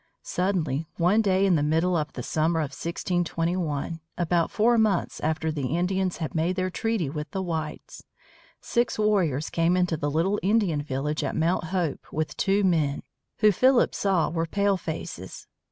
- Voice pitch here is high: No, medium, 170 Hz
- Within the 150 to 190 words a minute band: Yes, average, 165 wpm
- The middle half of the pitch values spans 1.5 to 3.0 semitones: No, average, 3.4 semitones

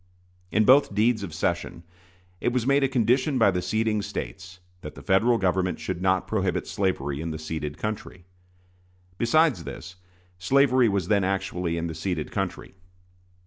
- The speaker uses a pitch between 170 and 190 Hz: No, very low, 95 Hz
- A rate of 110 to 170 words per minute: Yes, average, 160 wpm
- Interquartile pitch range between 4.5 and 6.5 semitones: Yes, average, 4.8 semitones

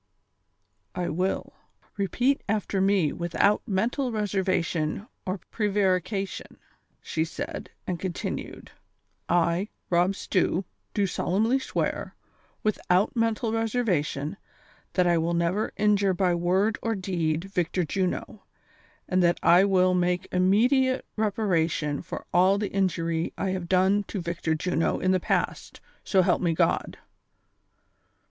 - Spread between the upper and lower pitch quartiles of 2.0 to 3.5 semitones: Yes, average, 3.0 semitones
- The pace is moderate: No, slow, 125 wpm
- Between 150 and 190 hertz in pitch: Yes, medium, 185 Hz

